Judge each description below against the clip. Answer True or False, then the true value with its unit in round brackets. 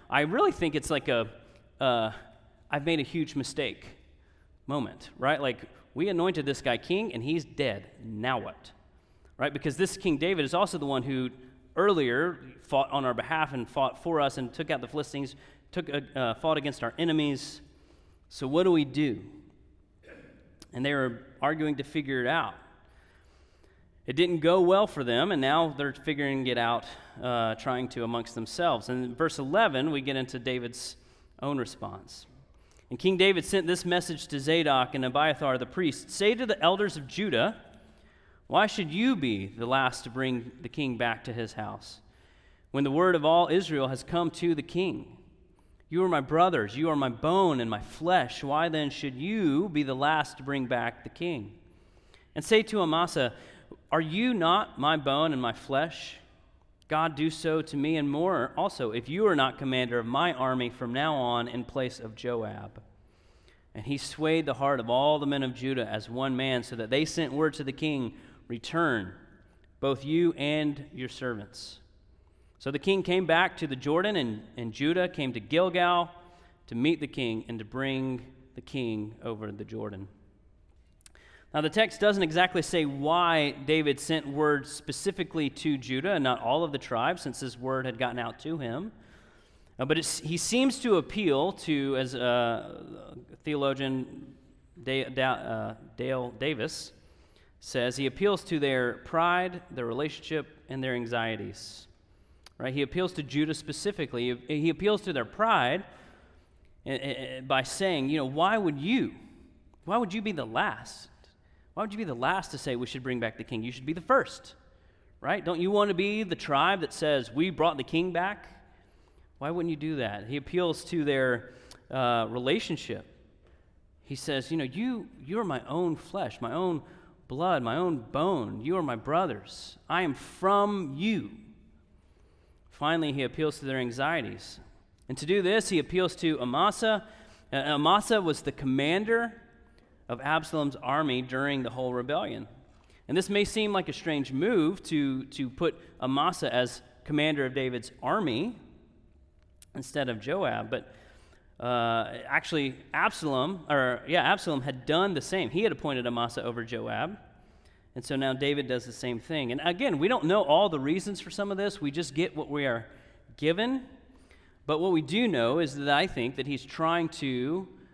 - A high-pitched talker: False (140 Hz)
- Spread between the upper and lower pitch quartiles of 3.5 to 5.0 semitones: False (5.5 semitones)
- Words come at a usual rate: True (180 wpm)